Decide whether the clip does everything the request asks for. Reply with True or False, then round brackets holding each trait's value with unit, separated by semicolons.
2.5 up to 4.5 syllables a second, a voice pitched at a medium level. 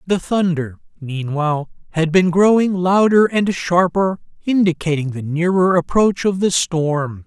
True (4.2 syllables/s; 175 Hz)